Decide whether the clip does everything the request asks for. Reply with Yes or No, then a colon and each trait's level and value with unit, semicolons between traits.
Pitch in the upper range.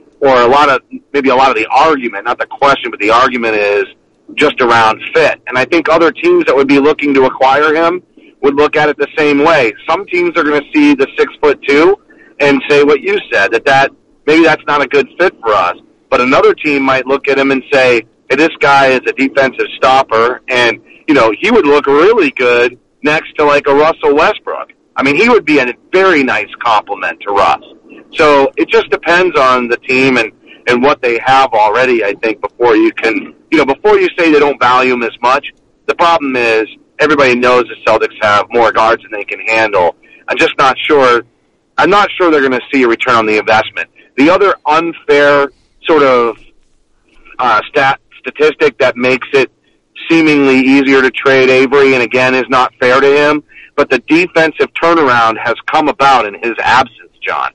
No: medium, 140 Hz